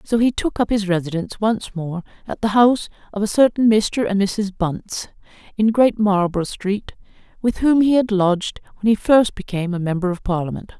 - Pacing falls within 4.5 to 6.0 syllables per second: Yes, 5.5 syllables/s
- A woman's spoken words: Yes, female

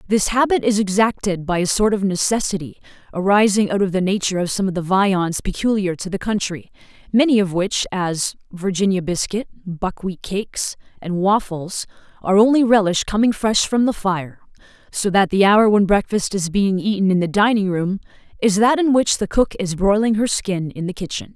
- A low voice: No, high, 195 Hz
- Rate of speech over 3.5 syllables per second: Yes, 5.2 syllables/s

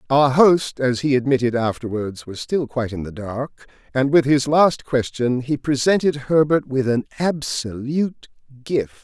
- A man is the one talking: Yes, male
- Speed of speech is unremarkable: Yes, average, 160 wpm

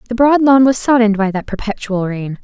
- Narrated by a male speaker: No, female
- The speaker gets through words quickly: Yes, fast, 220 wpm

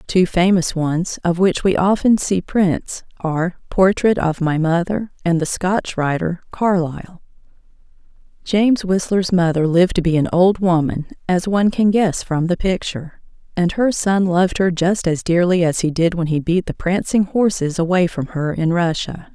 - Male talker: No, female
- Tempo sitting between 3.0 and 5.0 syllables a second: Yes, 4.7 syllables/s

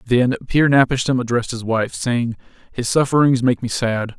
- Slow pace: No, average, 200 wpm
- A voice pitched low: Yes, low, 125 Hz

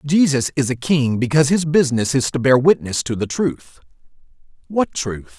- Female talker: No, male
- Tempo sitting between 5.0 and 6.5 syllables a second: Yes, 5.1 syllables/s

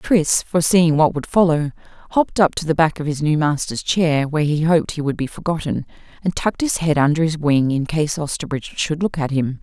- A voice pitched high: No, medium, 155 Hz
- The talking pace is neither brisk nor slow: No, fast, 225 wpm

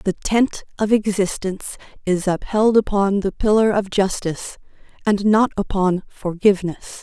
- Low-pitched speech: No, high, 200 Hz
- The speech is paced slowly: Yes, slow, 130 wpm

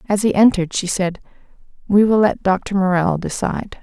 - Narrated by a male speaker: No, female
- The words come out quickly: No, average, 175 wpm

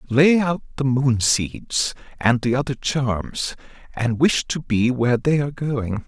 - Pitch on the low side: Yes, low, 130 Hz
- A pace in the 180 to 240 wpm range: No, average, 170 wpm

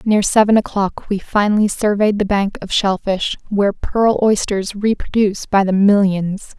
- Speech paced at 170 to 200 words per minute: No, average, 155 wpm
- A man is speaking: No, female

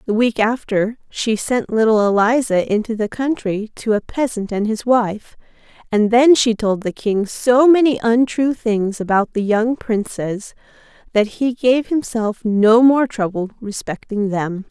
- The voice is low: No, high, 225 Hz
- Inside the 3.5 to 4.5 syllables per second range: Yes, 4.1 syllables/s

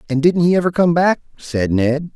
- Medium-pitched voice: Yes, medium, 155 Hz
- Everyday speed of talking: No, fast, 225 wpm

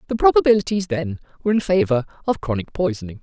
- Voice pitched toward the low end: No, medium, 170 Hz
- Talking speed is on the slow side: No, average, 165 wpm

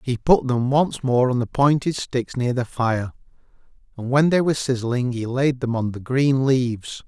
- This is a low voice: Yes, low, 130 Hz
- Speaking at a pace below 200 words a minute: No, fast, 205 wpm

